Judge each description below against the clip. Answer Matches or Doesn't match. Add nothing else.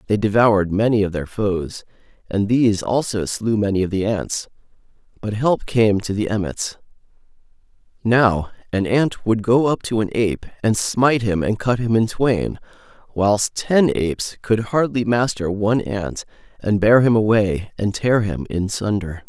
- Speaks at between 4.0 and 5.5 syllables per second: Matches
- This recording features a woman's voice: Doesn't match